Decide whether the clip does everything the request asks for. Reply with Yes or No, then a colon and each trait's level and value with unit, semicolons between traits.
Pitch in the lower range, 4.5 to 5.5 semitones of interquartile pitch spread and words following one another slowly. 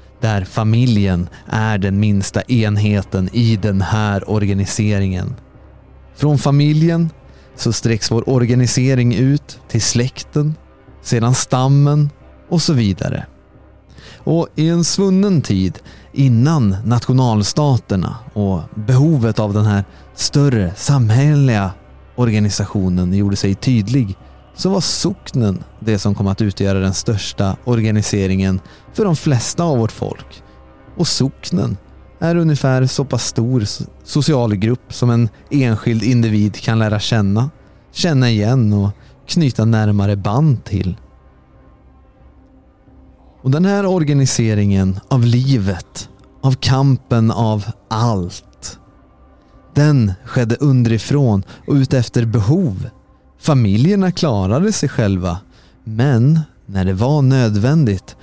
Yes: low, 115 Hz; average, 5.1 semitones; slow, 110 wpm